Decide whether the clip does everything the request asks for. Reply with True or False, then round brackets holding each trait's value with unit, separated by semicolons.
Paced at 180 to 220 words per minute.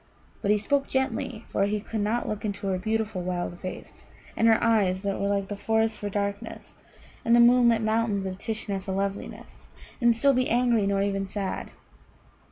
True (185 wpm)